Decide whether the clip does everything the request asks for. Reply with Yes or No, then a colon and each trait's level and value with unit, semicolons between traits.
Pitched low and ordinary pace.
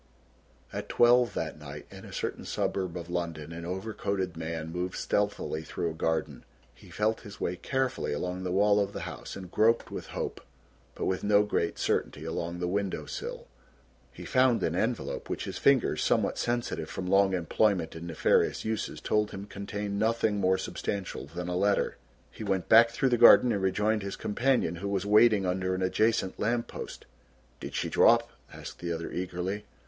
Yes: very low, 95 Hz; average, 185 wpm